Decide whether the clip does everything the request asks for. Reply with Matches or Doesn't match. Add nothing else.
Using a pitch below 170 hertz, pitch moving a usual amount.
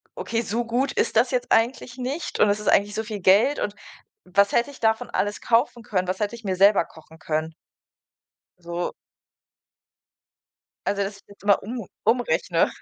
Doesn't match